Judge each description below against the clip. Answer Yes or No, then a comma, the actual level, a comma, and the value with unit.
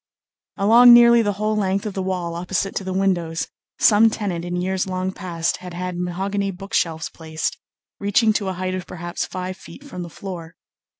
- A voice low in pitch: No, medium, 185 Hz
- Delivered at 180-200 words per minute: Yes, average, 190 wpm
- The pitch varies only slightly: Yes, narrow, 2.3 semitones